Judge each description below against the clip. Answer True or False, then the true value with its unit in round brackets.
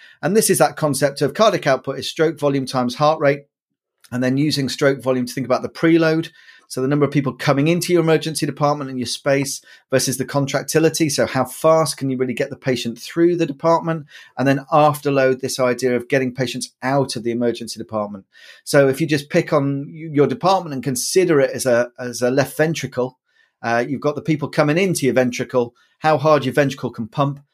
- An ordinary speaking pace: False (210 wpm)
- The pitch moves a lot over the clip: False (3.2 semitones)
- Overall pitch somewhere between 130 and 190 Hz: True (140 Hz)